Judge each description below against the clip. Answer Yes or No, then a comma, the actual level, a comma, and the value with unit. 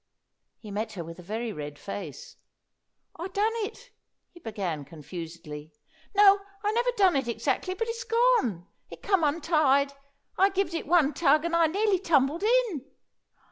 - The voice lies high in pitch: Yes, very high, 305 Hz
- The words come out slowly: No, average, 160 wpm